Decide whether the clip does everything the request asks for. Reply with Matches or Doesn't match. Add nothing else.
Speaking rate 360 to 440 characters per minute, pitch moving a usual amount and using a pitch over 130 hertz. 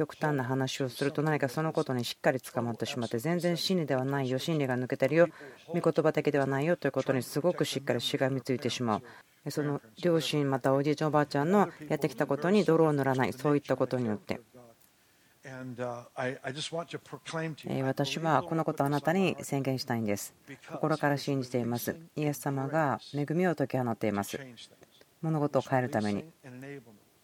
Matches